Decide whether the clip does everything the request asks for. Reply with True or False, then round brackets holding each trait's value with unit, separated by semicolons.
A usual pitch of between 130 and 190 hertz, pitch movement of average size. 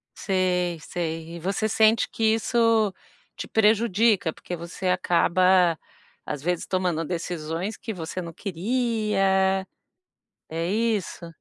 True (185 Hz; 4.1 semitones)